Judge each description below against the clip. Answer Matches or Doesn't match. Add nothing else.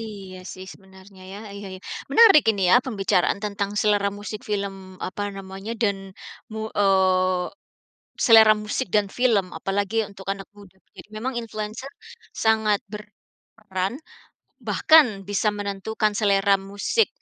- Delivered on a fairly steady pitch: Matches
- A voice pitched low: Doesn't match